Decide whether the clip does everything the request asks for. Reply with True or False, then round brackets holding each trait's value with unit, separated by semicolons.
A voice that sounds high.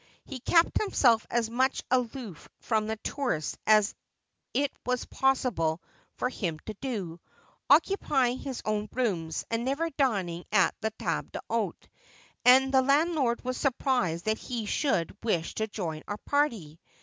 True (235 Hz)